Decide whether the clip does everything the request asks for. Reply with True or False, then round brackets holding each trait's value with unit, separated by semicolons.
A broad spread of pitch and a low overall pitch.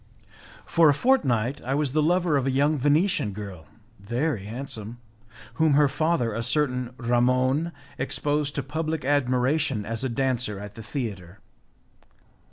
False (4.2 semitones; 130 Hz)